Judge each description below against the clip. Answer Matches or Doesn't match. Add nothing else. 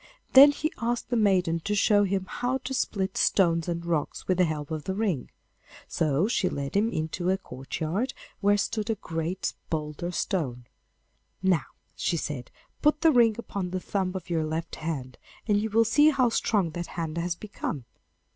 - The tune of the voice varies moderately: Matches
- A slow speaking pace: Doesn't match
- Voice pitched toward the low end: Doesn't match